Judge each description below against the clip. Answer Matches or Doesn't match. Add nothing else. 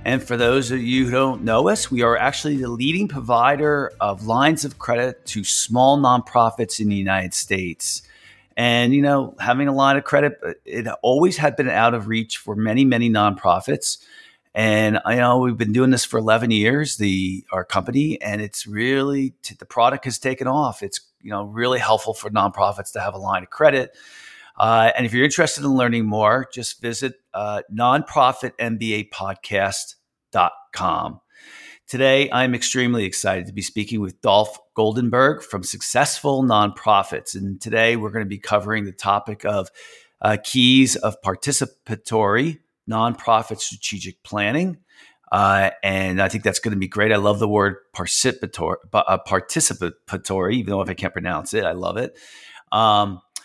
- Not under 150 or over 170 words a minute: Matches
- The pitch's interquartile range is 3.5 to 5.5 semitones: Matches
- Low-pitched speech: Matches